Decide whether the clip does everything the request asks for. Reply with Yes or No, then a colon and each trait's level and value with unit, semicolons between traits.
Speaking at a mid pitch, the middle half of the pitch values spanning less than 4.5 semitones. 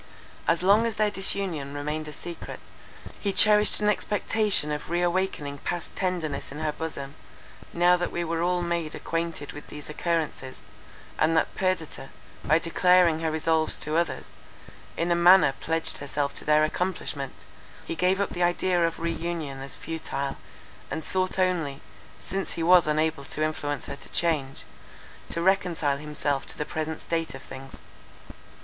Yes: medium, 165 Hz; average, 3.1 semitones